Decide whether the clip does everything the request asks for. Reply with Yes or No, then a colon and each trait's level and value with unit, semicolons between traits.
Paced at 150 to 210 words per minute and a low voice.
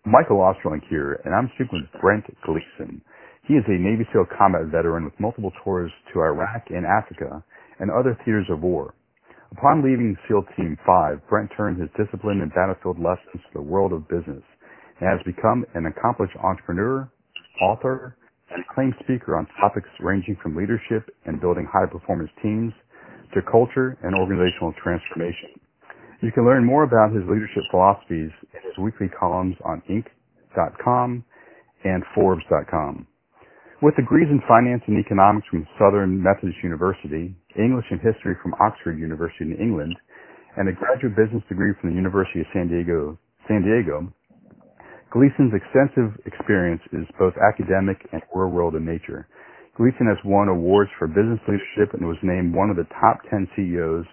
Yes: average, 160 wpm; low, 100 Hz